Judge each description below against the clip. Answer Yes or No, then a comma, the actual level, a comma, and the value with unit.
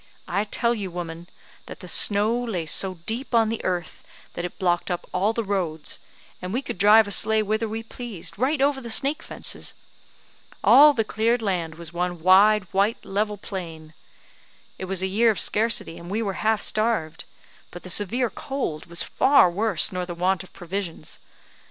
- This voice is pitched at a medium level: No, high, 200 Hz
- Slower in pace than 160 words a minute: No, average, 185 wpm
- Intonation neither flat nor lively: Yes, average, 4.2 semitones